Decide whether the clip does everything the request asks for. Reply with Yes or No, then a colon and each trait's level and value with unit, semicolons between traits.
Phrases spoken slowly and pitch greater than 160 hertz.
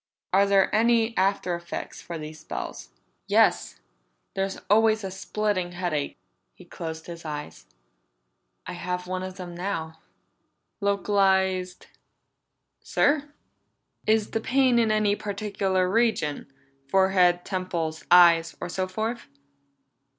Yes: slow, 115 wpm; high, 190 Hz